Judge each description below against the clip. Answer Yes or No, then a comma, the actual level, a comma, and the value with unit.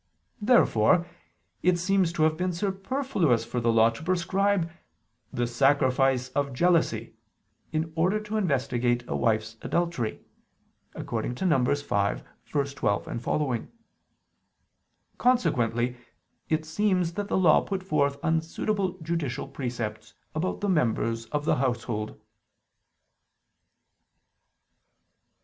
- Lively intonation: Yes, wide, 6.9 semitones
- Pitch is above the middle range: No, medium, 150 Hz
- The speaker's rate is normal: No, slow, 100 wpm